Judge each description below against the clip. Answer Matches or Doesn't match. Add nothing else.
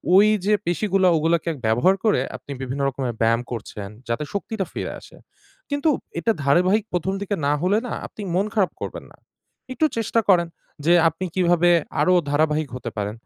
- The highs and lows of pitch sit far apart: Matches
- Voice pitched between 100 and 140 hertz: Doesn't match